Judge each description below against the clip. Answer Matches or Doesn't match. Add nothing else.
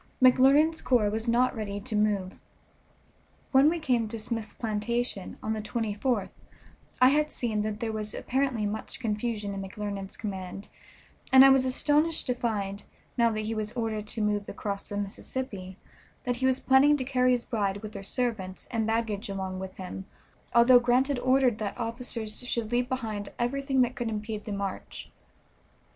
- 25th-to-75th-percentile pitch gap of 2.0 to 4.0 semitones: Matches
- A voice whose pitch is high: Matches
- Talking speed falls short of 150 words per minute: Doesn't match